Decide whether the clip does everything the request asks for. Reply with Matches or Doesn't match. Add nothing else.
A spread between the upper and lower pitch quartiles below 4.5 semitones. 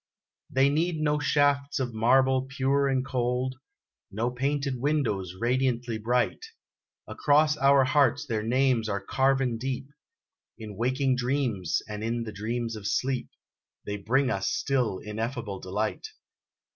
Matches